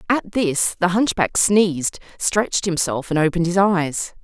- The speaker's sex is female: Yes, female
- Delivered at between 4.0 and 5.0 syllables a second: Yes, 4.5 syllables/s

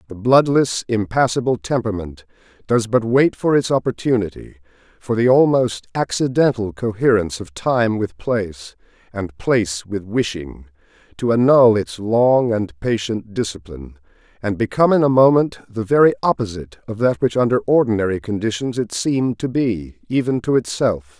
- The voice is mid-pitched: No, low, 110 Hz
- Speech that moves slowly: No, average, 145 wpm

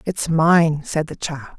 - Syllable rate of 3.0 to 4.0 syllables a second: Yes, 3.9 syllables/s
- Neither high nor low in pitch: Yes, medium, 165 Hz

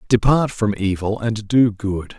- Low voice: Yes, low, 110 Hz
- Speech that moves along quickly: No, average, 165 wpm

